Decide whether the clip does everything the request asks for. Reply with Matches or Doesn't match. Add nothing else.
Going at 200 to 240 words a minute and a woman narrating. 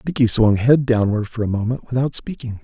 Doesn't match